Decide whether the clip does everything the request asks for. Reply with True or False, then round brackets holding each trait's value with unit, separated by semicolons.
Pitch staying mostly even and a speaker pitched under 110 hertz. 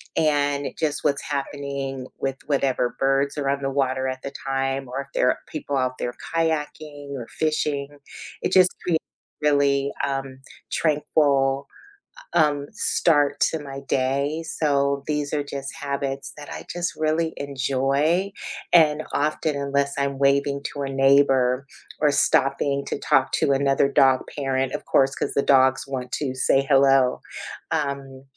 False (1.4 semitones; 140 Hz)